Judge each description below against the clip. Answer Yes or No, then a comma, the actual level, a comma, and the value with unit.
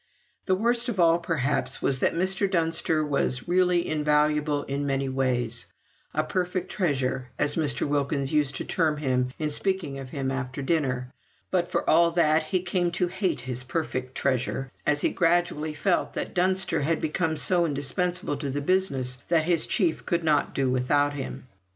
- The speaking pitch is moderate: Yes, medium, 150 Hz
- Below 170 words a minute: No, average, 175 wpm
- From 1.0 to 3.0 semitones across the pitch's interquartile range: No, average, 4.4 semitones